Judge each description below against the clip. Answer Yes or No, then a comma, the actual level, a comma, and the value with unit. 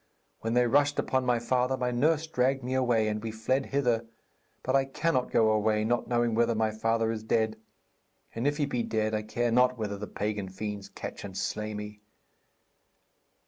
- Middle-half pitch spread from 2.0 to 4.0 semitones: Yes, average, 2.9 semitones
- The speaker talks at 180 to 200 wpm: Yes, average, 190 wpm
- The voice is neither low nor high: No, low, 115 Hz